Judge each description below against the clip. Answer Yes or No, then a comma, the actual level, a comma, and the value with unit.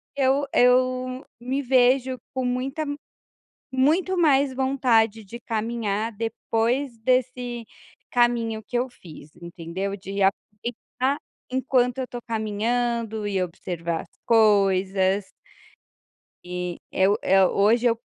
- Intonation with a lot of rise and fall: No, average, 4.1 semitones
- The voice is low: No, high, 235 Hz